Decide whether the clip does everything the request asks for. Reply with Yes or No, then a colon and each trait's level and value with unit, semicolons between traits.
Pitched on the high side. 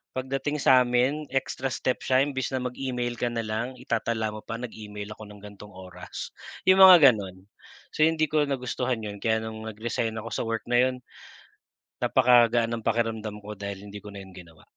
No: low, 115 Hz